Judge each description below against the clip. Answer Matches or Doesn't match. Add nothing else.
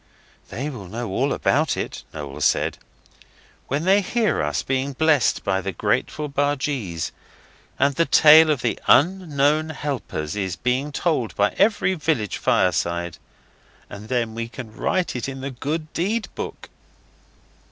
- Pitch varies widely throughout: Matches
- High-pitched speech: Doesn't match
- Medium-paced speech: Matches